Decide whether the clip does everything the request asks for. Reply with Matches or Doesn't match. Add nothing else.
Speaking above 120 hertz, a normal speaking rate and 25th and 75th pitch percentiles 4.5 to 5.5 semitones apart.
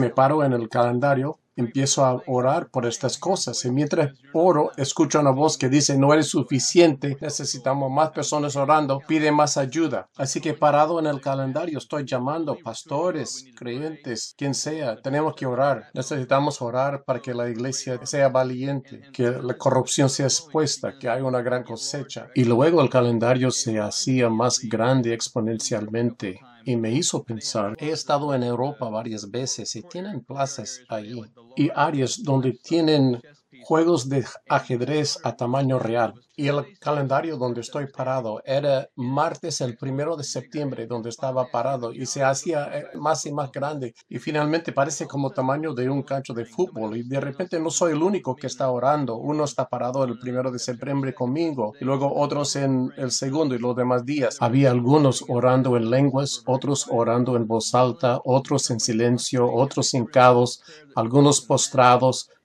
Doesn't match